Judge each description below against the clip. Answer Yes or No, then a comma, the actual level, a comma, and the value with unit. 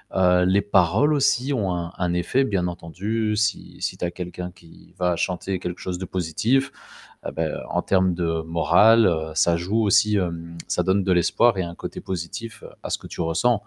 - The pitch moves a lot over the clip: No, average, 3.7 semitones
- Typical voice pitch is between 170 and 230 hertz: No, very low, 90 Hz